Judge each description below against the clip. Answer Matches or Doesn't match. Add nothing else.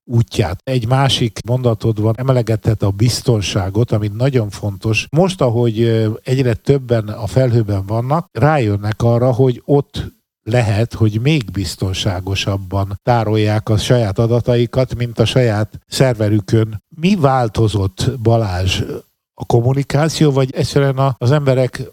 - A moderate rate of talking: Matches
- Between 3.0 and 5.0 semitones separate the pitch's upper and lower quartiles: Matches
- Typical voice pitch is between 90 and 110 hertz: Doesn't match